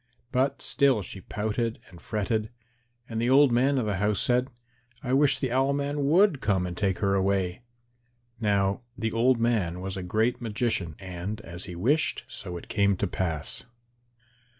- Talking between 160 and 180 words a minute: Yes, average, 175 wpm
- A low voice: Yes, low, 110 Hz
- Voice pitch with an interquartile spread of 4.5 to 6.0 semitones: Yes, average, 4.8 semitones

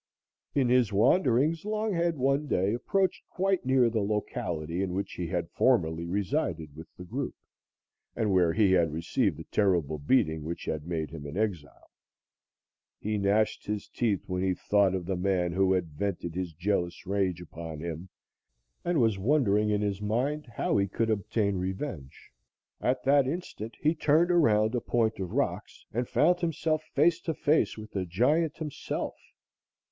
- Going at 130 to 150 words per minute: No, average, 165 wpm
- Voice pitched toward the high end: No, low, 105 Hz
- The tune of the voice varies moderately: No, wide, 7.0 semitones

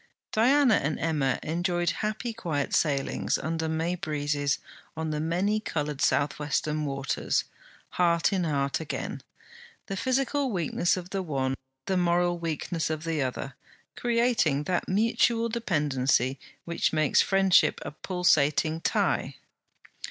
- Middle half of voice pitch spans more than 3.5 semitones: Yes, average, 4.6 semitones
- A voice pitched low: No, medium, 165 Hz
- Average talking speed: No, slow, 130 wpm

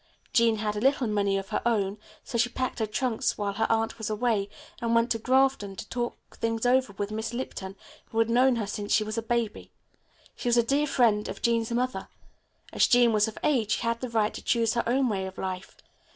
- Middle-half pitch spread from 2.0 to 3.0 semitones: Yes, narrow, 2.4 semitones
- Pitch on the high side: Yes, high, 230 Hz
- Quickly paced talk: Yes, fast, 230 wpm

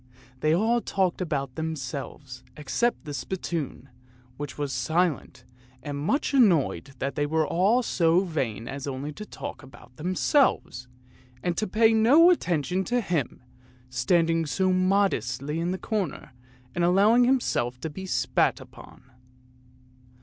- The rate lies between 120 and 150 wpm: Yes, slow, 135 wpm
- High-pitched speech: No, medium, 165 Hz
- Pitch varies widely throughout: Yes, wide, 5.7 semitones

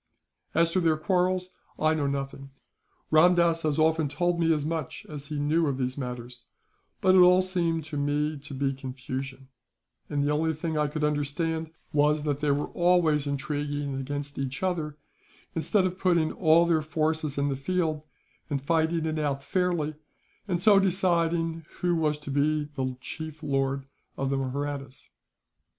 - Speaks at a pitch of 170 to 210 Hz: No, medium, 150 Hz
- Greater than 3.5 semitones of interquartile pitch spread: No, average, 2.7 semitones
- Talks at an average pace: Yes, average, 170 wpm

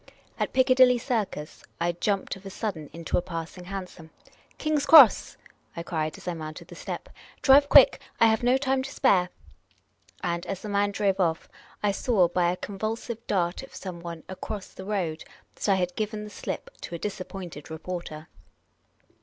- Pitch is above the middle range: Yes, high, 195 Hz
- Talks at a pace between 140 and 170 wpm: No, average, 185 wpm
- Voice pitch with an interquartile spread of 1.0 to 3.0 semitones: No, average, 4.3 semitones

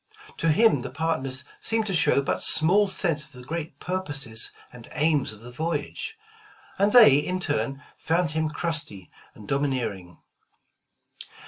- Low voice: No, medium, 150 Hz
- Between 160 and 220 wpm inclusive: No, average, 145 wpm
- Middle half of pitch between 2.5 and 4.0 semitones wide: No, average, 4.4 semitones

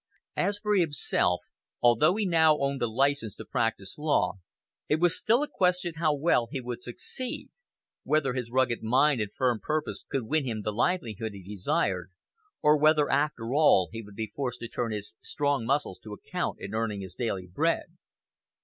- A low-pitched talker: Yes, low, 130 Hz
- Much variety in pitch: Yes, wide, 5.8 semitones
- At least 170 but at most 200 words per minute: Yes, average, 180 wpm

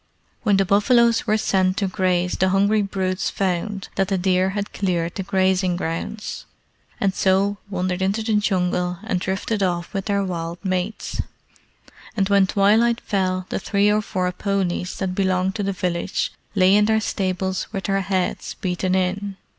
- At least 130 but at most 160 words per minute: No, average, 170 wpm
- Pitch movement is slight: Yes, narrow, 1.6 semitones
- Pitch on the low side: No, high, 190 Hz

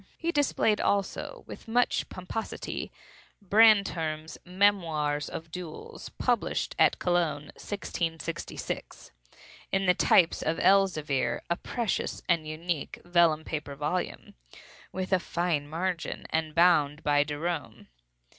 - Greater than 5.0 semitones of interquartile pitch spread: No, average, 3.4 semitones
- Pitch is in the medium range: Yes, medium, 170 Hz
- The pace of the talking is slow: Yes, slow, 110 wpm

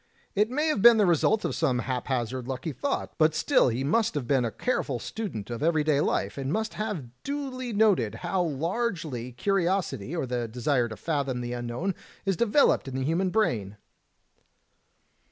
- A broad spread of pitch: Yes, wide, 8.6 semitones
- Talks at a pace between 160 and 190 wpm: Yes, average, 175 wpm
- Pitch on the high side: No, medium, 155 Hz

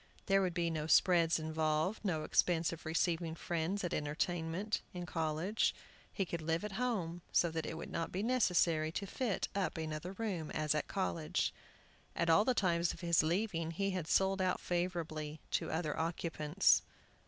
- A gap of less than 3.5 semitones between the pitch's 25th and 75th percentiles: Yes, average, 2.8 semitones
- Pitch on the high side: No, medium, 170 Hz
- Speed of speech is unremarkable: Yes, average, 175 wpm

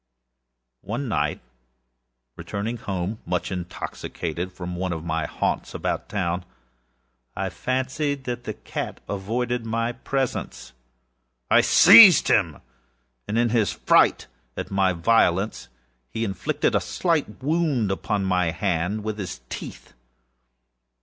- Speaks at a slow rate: Yes, slow, 120 wpm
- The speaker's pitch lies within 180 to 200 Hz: No, low, 105 Hz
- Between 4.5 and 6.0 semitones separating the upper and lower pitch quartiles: Yes, average, 5.2 semitones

